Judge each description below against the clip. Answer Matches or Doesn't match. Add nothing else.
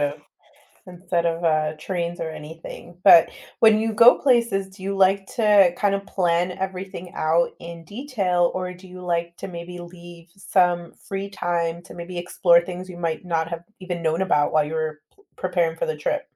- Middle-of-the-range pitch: Matches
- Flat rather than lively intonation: Matches